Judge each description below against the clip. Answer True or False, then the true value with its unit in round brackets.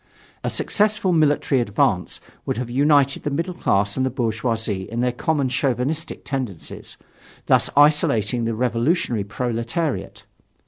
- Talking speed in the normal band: False (130 wpm)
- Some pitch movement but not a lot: True (4.4 semitones)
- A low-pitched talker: True (125 Hz)